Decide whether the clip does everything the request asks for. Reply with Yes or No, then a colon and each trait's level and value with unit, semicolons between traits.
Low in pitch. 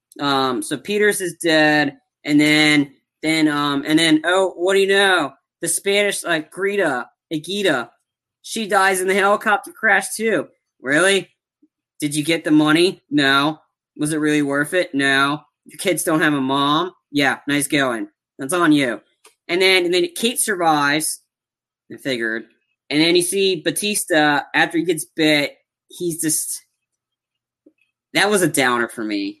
No: medium, 160 Hz